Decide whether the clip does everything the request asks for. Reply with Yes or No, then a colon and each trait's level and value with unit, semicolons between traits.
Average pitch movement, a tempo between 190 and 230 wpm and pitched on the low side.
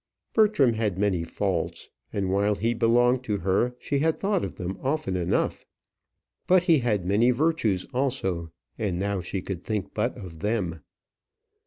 No: average, 5.0 semitones; average, 160 wpm; low, 105 Hz